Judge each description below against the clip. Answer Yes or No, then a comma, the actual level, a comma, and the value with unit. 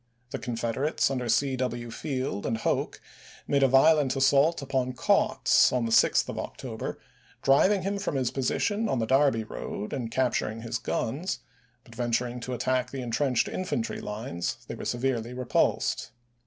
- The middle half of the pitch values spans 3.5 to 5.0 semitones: No, average, 2.8 semitones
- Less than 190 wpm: Yes, average, 160 wpm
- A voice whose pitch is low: Yes, low, 130 Hz